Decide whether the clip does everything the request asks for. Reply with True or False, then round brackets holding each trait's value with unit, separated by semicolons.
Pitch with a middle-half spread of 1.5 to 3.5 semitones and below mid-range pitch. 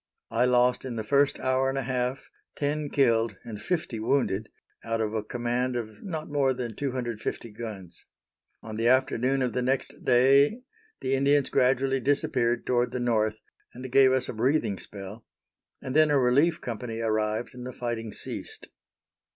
True (2.9 semitones; 125 Hz)